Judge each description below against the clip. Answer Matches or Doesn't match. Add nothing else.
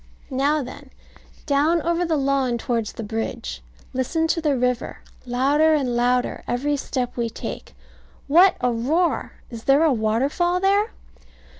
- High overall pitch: Matches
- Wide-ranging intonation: Doesn't match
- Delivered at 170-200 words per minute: Doesn't match